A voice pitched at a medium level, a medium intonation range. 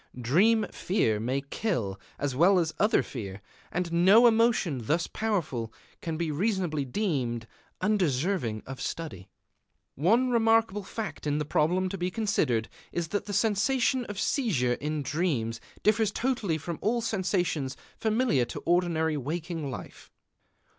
No: medium, 170 Hz; wide, 7.2 semitones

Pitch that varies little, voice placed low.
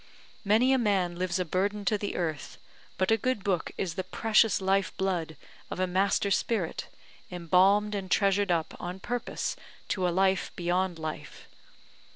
No: narrow, 2.3 semitones; high, 190 Hz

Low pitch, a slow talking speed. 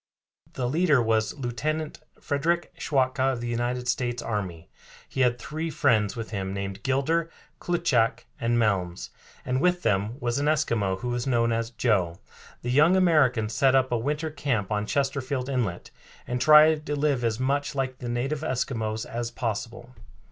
No: low, 125 Hz; average, 165 wpm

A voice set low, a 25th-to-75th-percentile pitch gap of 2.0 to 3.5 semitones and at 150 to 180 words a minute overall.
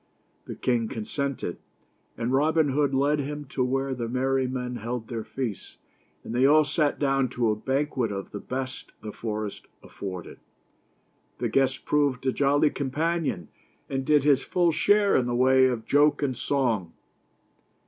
Yes: low, 130 Hz; average, 3.1 semitones; average, 160 wpm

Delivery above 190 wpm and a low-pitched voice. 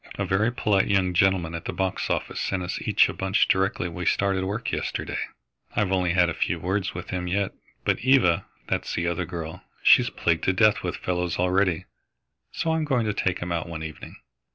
Yes: fast, 205 wpm; very low, 95 Hz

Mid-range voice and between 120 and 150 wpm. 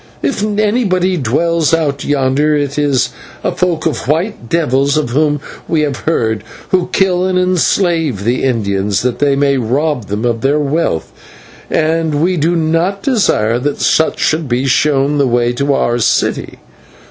No: medium, 145 Hz; average, 160 wpm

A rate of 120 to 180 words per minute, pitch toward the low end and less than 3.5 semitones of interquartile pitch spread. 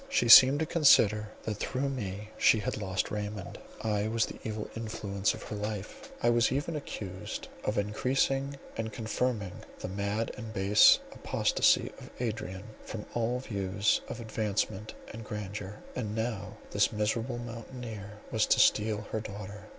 Yes: average, 155 wpm; low, 110 Hz; narrow, 2.4 semitones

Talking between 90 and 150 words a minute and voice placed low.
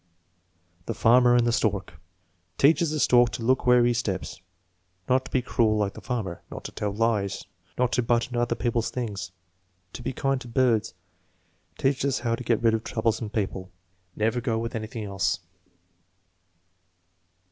No: average, 170 wpm; low, 115 Hz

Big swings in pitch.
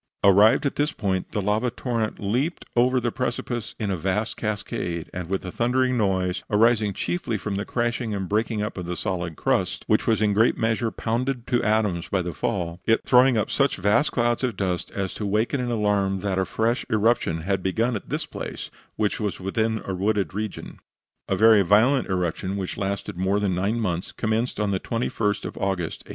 No: average, 3.4 semitones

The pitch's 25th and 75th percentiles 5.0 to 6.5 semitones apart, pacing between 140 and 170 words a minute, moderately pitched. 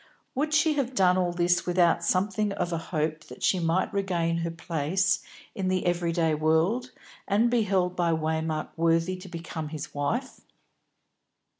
No: average, 2.9 semitones; average, 165 wpm; medium, 175 Hz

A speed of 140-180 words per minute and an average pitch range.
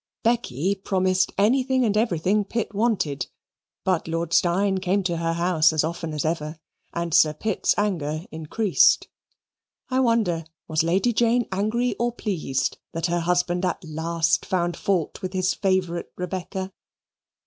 Yes: average, 145 wpm; average, 3.7 semitones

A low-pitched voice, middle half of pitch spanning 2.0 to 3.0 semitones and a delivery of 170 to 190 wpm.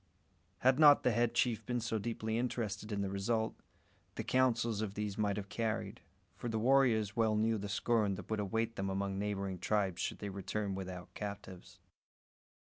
Yes: low, 105 Hz; narrow, 2.6 semitones; average, 180 wpm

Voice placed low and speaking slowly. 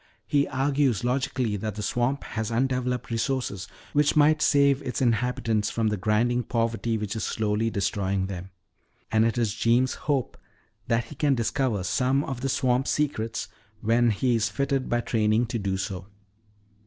No: low, 120 Hz; average, 165 wpm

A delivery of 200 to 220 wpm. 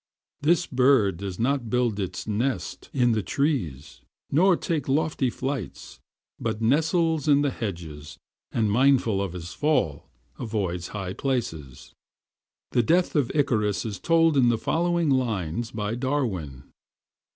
No: slow, 135 wpm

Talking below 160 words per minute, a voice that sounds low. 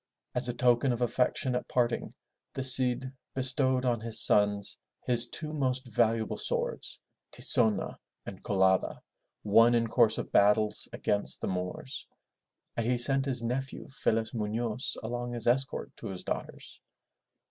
Yes: average, 150 wpm; low, 120 Hz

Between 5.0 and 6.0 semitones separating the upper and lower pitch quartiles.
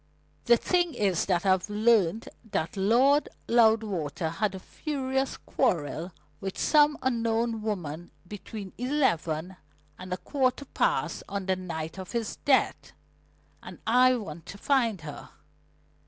Yes: average, 5.3 semitones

